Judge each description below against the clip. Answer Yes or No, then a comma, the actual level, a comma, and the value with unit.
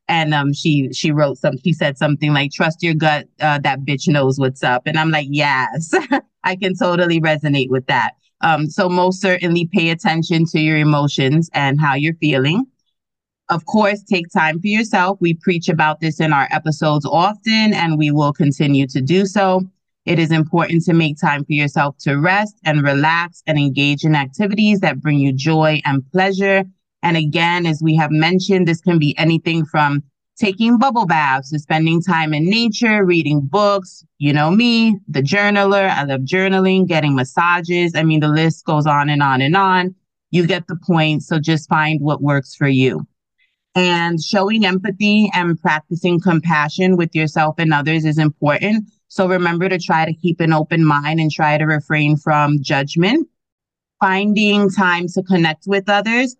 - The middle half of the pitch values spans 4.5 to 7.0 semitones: No, average, 3.8 semitones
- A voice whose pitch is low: No, medium, 165 Hz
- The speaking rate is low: No, average, 180 wpm